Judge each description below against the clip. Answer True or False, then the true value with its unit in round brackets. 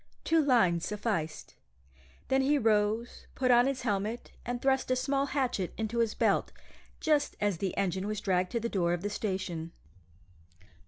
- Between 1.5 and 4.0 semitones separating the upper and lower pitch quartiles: False (5.1 semitones)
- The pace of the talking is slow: False (165 wpm)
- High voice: True (220 Hz)